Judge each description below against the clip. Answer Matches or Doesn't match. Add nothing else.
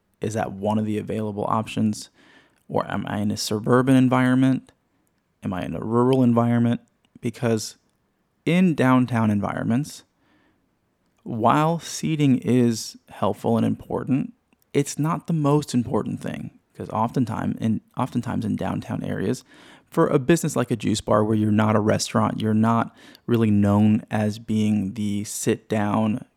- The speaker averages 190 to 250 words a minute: Doesn't match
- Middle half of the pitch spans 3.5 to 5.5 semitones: Doesn't match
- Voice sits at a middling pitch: Doesn't match